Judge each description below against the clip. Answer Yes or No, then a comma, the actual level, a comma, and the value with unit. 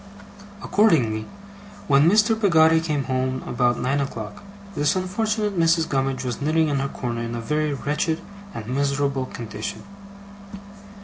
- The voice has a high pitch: No, medium, 140 Hz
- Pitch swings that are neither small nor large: Yes, average, 4.3 semitones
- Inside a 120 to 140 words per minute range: Yes, slow, 135 wpm